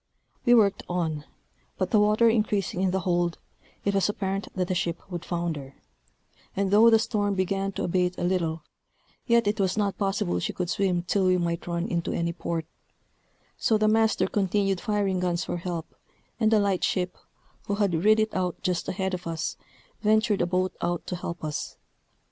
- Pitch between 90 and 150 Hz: No, medium, 185 Hz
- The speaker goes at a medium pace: Yes, average, 190 wpm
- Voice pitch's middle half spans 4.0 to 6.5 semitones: No, average, 2.9 semitones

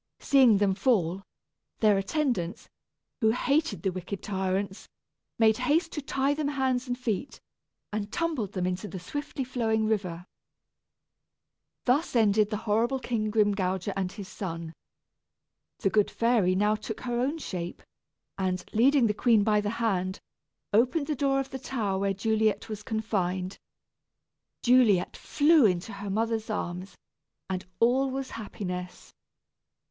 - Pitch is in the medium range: No, high, 215 Hz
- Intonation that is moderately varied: Yes, average, 4.6 semitones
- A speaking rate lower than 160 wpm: Yes, average, 140 wpm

